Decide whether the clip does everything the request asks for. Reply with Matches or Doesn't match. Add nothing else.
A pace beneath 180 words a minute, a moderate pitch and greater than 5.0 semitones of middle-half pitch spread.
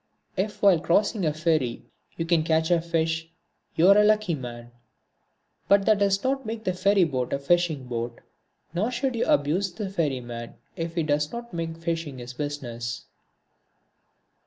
Matches